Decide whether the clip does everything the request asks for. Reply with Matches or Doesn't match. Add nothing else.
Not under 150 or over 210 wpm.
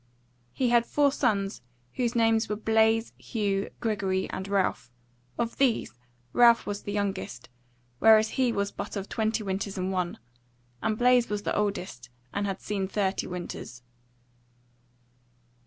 Doesn't match